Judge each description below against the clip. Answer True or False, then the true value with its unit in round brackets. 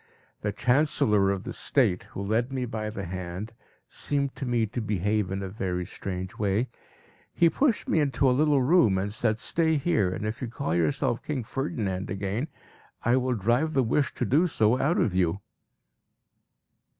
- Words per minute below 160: False (180 wpm)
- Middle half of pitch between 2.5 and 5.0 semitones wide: False (5.5 semitones)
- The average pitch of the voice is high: False (115 Hz)